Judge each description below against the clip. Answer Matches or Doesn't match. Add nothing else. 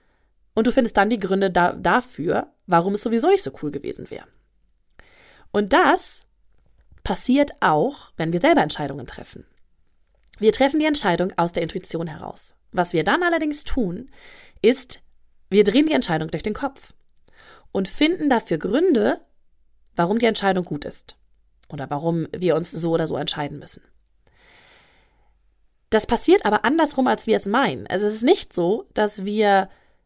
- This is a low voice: Doesn't match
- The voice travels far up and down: Matches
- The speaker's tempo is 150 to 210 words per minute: Matches